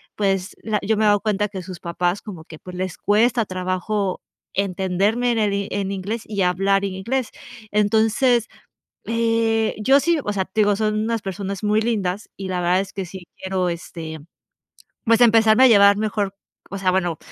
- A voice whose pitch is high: Yes, high, 200 Hz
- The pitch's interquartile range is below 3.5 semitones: Yes, average, 2.8 semitones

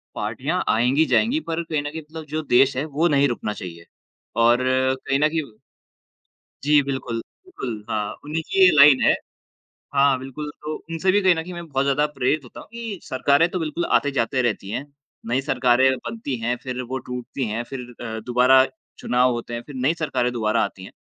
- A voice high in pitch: No, low, 135 Hz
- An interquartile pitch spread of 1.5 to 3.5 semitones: No, average, 3.9 semitones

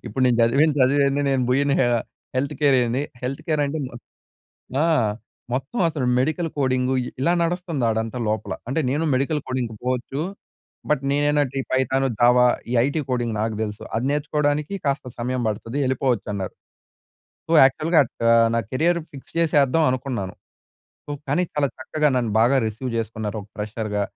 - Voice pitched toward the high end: No, low, 130 Hz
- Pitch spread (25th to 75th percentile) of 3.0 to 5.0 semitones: Yes, average, 3.5 semitones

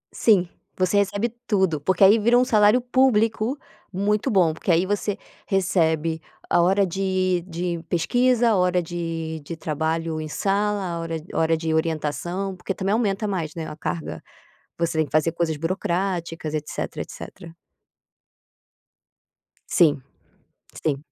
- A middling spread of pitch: Yes, average, 3.8 semitones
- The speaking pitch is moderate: Yes, medium, 180 Hz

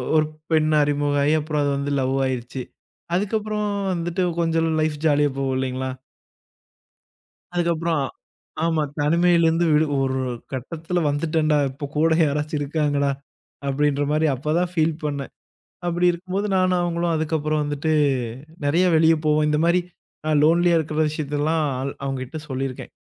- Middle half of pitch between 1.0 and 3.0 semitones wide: Yes, narrow, 2.6 semitones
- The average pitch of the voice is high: No, medium, 155 Hz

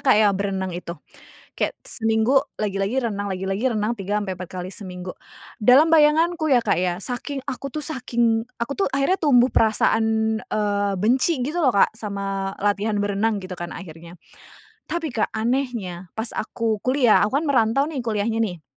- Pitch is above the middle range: Yes, high, 220 Hz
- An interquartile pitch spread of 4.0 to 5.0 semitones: Yes, average, 4.6 semitones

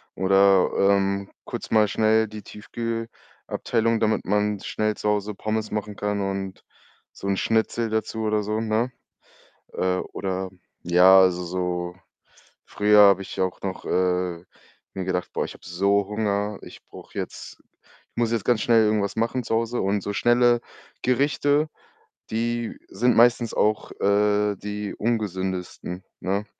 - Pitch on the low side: Yes, low, 105 Hz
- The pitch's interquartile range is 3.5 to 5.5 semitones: No, narrow, 2.5 semitones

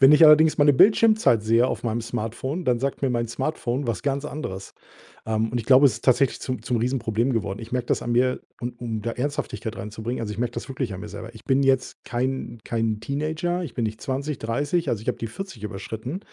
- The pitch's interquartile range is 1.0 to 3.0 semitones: No, average, 3.7 semitones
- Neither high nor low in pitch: No, low, 125 Hz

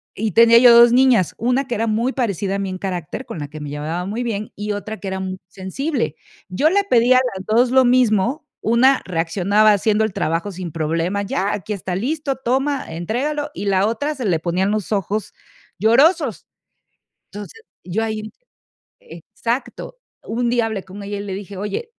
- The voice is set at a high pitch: Yes, high, 215 Hz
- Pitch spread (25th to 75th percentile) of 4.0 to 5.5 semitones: Yes, average, 4.5 semitones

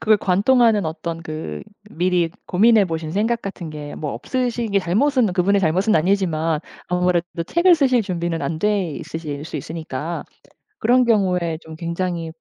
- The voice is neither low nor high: Yes, medium, 180 Hz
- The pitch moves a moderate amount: Yes, average, 4.5 semitones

